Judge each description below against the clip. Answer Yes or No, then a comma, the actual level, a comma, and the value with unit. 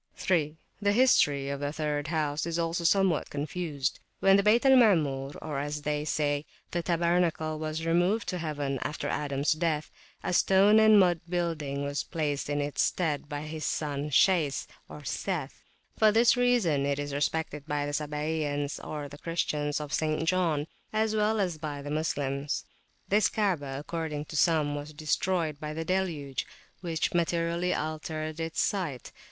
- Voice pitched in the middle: Yes, medium, 155 Hz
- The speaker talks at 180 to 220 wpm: No, average, 165 wpm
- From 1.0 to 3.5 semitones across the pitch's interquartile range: Yes, average, 3.2 semitones